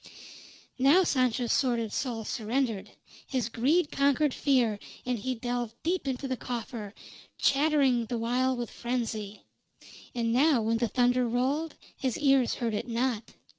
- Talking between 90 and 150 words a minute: Yes, average, 140 wpm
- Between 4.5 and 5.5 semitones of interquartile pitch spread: No, average, 2.8 semitones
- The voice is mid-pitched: No, high, 245 Hz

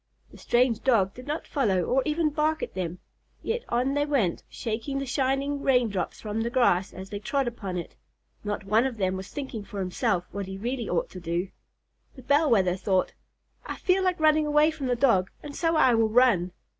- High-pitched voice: Yes, high, 240 Hz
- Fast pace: Yes, fast, 210 wpm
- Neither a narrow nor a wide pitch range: No, wide, 6.5 semitones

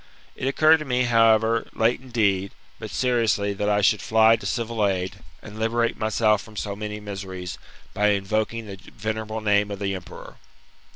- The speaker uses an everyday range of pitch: No, narrow, 2.2 semitones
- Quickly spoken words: No, average, 170 wpm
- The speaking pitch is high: No, low, 110 Hz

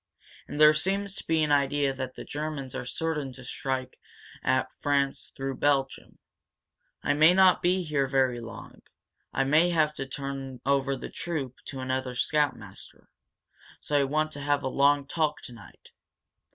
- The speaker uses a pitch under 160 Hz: Yes, medium, 140 Hz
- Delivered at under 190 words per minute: Yes, average, 165 wpm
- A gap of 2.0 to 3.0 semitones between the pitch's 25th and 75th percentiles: Yes, narrow, 2.5 semitones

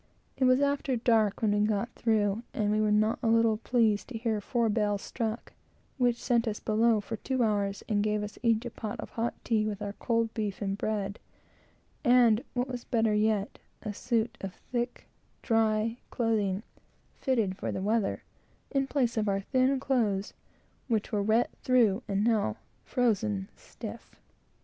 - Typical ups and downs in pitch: No, narrow, 2.3 semitones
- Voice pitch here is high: Yes, high, 220 Hz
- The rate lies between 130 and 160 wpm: No, average, 175 wpm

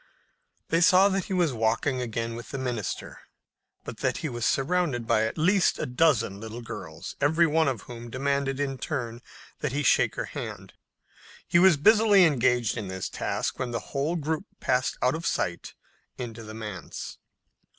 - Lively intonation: Yes, wide, 5.7 semitones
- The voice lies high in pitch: No, low, 130 Hz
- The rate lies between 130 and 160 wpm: No, average, 175 wpm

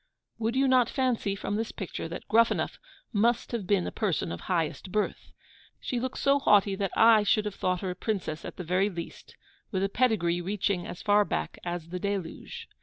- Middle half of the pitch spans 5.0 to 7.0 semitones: No, average, 3.9 semitones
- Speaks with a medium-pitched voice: No, high, 200 Hz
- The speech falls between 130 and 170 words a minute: No, average, 200 wpm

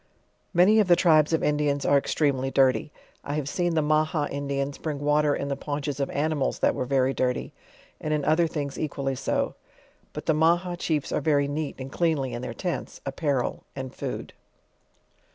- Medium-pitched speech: Yes, medium, 145 Hz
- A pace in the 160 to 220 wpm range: Yes, average, 180 wpm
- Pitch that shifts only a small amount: Yes, narrow, 2.3 semitones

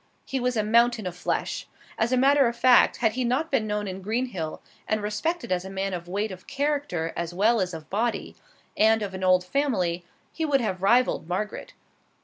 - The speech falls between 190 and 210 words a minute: Yes, fast, 205 wpm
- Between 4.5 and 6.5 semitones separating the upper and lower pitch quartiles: Yes, average, 5.1 semitones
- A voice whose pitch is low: No, high, 215 Hz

